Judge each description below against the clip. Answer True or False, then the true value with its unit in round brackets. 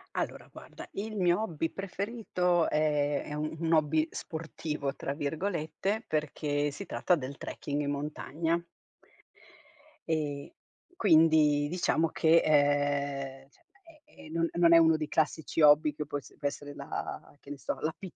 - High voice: False (155 Hz)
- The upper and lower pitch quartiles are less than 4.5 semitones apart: True (2.5 semitones)